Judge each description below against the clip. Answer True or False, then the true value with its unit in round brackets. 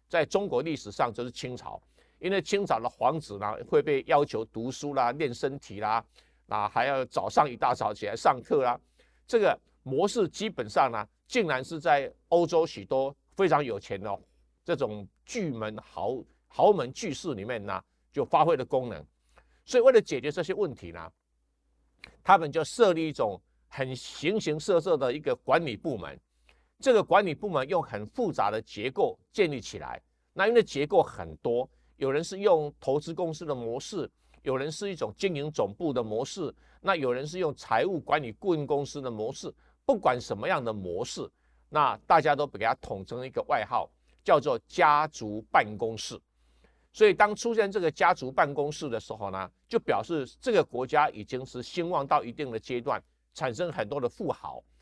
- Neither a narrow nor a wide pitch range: False (8.0 semitones)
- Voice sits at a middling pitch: True (145 Hz)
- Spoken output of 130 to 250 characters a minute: False (265 characters per minute)